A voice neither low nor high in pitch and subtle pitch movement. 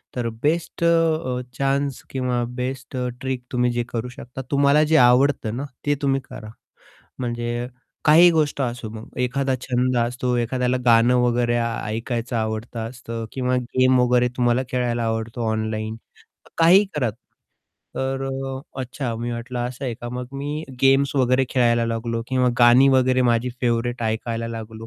No: low, 125 Hz; narrow, 2.1 semitones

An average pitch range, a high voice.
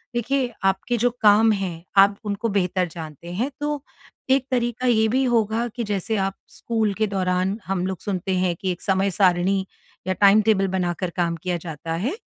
Yes: average, 3.7 semitones; high, 195 Hz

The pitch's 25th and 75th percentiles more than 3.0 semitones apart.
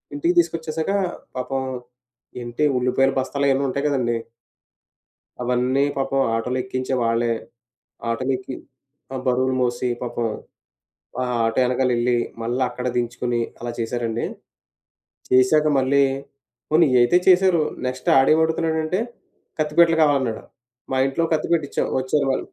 Yes: average, 3.6 semitones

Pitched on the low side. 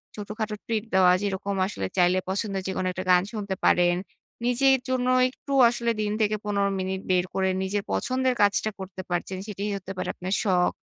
No: high, 200 Hz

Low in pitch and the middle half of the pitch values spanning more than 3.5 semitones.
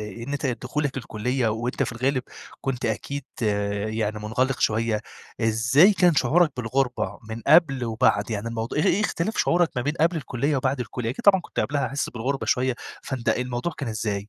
Yes: low, 125 Hz; average, 4.0 semitones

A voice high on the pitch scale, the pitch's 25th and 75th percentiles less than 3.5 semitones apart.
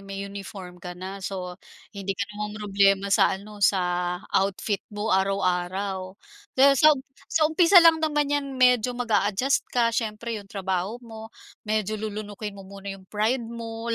Yes: high, 205 Hz; average, 3.1 semitones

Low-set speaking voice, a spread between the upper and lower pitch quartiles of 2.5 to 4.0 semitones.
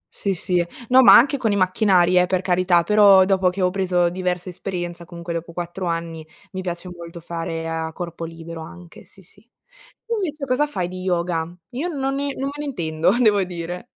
No: medium, 180 Hz; average, 2.8 semitones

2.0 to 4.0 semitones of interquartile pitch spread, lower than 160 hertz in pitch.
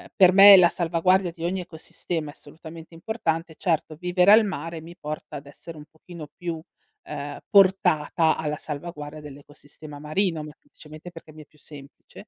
No: average, 2.7 semitones; medium, 165 Hz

